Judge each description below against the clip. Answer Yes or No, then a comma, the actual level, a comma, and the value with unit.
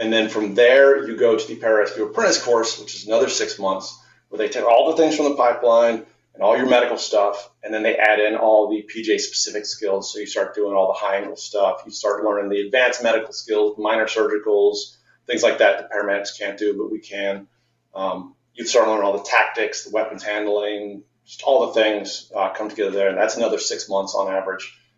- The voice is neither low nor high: No, low, 110 Hz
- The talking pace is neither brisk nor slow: No, fast, 225 wpm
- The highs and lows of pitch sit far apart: Yes, wide, 7.9 semitones